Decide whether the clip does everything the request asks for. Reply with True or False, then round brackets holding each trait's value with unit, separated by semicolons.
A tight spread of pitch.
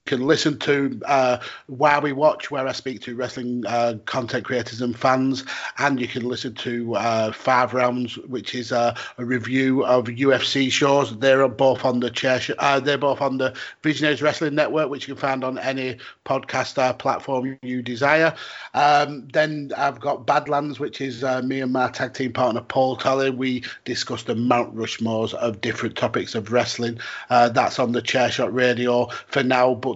True (2.1 semitones)